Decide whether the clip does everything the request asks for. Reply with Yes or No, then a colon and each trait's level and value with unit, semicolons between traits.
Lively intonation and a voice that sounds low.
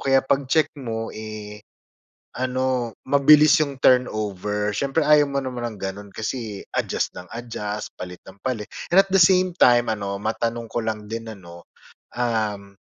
No: average, 4.2 semitones; low, 115 Hz